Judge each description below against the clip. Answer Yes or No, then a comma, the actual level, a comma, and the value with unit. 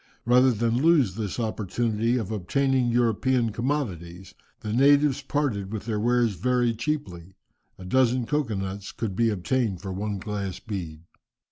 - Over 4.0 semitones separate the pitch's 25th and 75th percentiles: Yes, average, 4.4 semitones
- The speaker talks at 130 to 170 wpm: Yes, average, 145 wpm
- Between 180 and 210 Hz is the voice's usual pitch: No, low, 115 Hz